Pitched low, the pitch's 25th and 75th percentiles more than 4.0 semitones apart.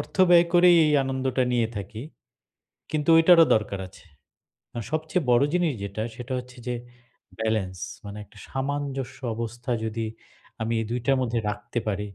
Yes: low, 125 Hz; average, 4.6 semitones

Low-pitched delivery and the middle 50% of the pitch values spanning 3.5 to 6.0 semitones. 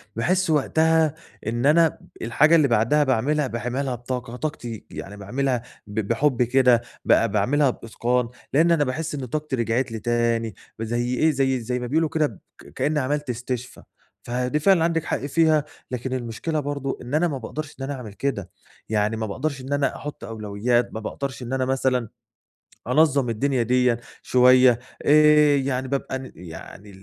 Yes: low, 130 Hz; average, 3.8 semitones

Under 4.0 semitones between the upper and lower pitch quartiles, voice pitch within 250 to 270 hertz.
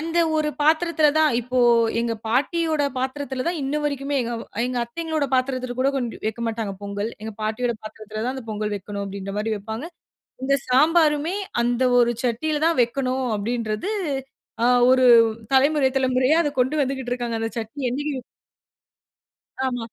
No: average, 4.3 semitones; very high, 255 Hz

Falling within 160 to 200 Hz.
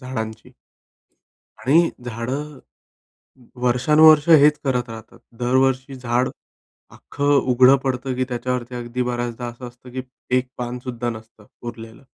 No: low, 125 Hz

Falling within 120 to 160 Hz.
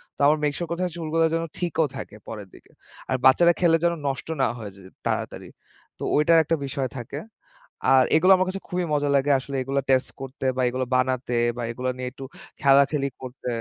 Yes: medium, 140 Hz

